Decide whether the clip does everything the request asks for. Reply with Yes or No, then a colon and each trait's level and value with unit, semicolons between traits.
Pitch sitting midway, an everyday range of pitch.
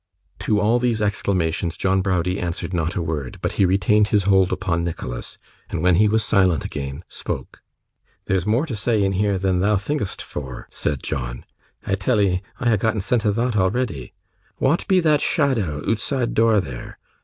No: very low, 95 Hz; average, 4.2 semitones